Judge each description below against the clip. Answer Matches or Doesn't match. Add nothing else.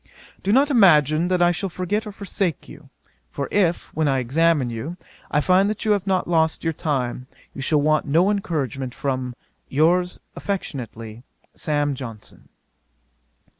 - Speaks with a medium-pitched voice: Matches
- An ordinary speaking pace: Matches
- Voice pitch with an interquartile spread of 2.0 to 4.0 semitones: Doesn't match